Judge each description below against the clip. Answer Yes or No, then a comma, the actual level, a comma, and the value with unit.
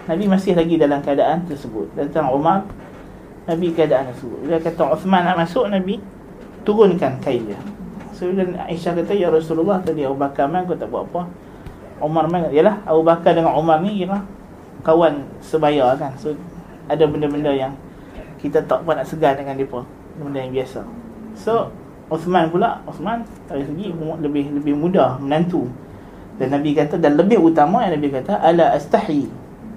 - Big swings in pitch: No, average, 4.0 semitones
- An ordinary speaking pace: No, fast, 165 wpm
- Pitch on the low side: No, medium, 160 Hz